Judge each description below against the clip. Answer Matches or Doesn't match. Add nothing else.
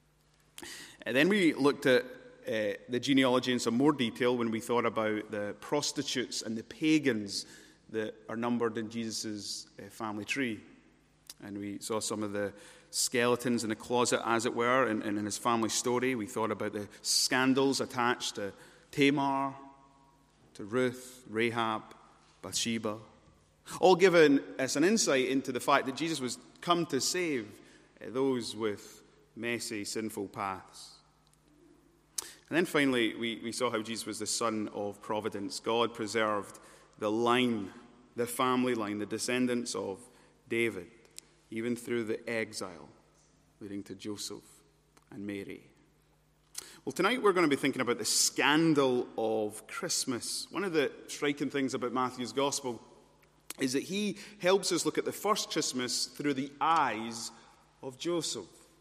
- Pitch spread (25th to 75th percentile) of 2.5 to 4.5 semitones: Matches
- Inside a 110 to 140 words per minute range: Doesn't match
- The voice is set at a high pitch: Doesn't match